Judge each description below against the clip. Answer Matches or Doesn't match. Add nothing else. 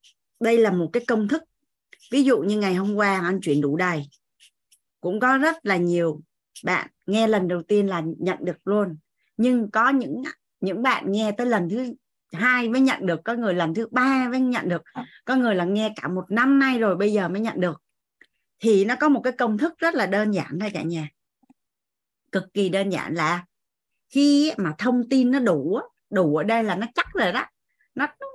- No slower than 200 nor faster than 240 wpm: Matches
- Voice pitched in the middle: Doesn't match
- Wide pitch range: Matches